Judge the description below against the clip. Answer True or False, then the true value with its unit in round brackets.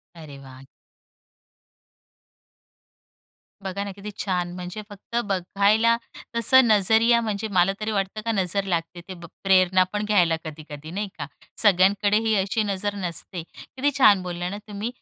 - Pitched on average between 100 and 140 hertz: False (195 Hz)